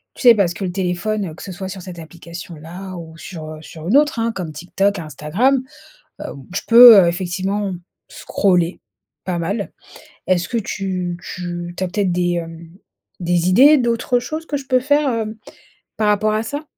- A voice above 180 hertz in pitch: Yes, high, 190 Hz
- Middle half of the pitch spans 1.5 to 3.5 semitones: No, average, 4.2 semitones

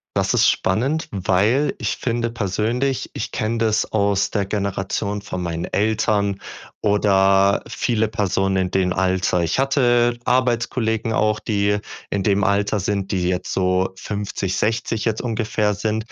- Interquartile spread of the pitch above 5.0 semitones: No, average, 2.7 semitones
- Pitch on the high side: No, low, 105 Hz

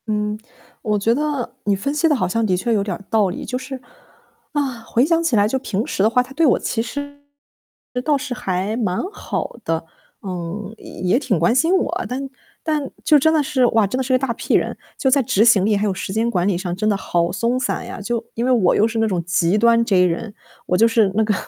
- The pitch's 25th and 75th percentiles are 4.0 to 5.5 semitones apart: Yes, average, 4.7 semitones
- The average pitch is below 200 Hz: No, high, 225 Hz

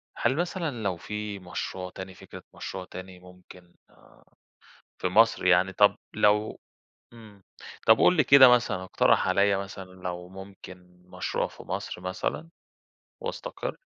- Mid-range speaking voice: No, very low, 95 Hz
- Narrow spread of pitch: No, average, 3.4 semitones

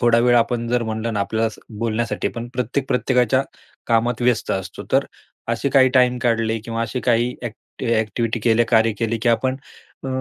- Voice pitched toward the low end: Yes, low, 115 Hz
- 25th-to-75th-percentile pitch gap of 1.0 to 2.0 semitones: Yes, narrow, 1.5 semitones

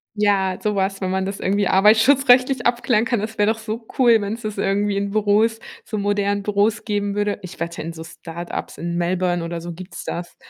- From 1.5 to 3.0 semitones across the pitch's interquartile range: Yes, average, 2.7 semitones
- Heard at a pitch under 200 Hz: No, high, 205 Hz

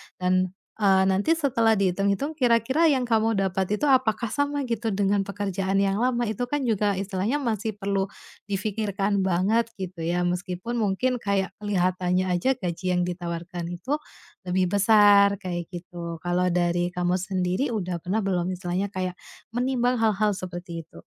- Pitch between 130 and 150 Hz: No, high, 195 Hz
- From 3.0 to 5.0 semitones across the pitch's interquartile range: Yes, average, 3.7 semitones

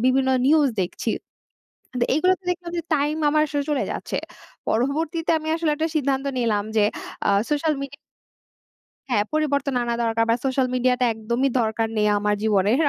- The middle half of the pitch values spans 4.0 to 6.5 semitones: Yes, average, 5.0 semitones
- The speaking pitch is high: Yes, very high, 270 Hz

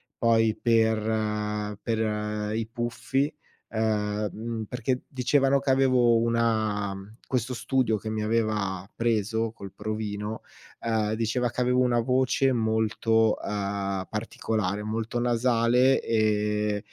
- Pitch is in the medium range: No, low, 110 Hz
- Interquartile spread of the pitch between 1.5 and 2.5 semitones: Yes, narrow, 1.9 semitones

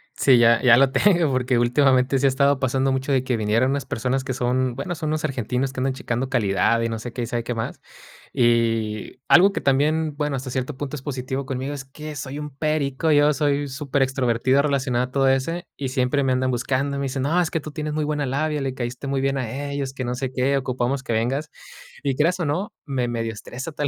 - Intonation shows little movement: Yes, narrow, 2.3 semitones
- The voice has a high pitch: No, low, 135 Hz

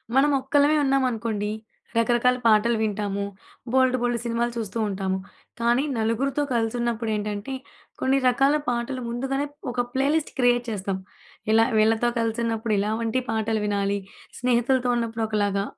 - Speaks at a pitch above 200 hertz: Yes, high, 235 Hz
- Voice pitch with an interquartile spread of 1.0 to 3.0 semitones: Yes, narrow, 2.6 semitones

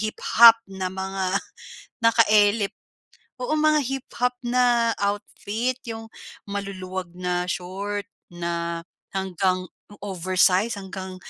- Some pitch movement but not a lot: Yes, average, 3.5 semitones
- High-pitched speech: Yes, high, 200 Hz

